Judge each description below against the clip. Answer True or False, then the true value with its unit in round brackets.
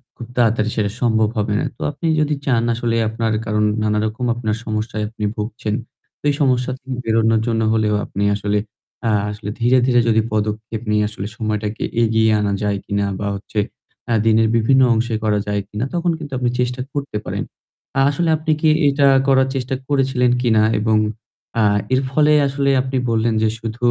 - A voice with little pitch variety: False (3.3 semitones)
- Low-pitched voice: True (115 Hz)